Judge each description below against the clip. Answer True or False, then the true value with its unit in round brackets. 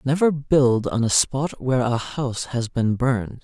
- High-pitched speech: False (130 Hz)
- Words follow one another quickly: False (190 wpm)